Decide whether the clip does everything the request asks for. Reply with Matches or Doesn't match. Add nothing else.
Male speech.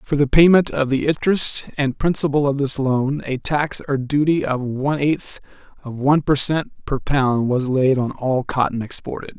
Matches